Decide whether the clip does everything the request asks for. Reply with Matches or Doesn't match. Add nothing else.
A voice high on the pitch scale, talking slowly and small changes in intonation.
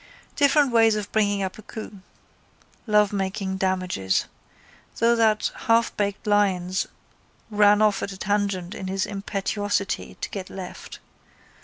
Matches